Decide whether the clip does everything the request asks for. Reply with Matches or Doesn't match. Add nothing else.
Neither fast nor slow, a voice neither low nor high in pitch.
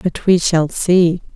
Matches